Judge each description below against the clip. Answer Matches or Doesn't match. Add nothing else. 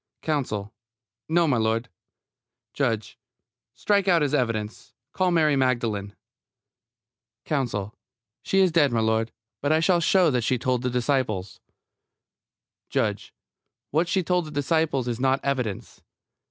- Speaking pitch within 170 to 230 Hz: Doesn't match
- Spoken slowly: Matches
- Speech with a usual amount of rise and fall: Doesn't match